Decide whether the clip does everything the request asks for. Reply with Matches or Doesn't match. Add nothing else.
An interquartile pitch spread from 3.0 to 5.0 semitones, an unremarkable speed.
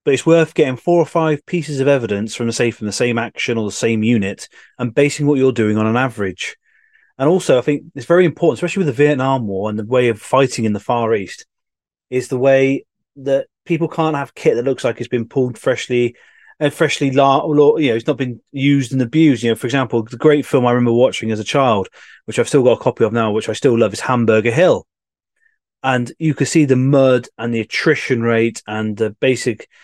Doesn't match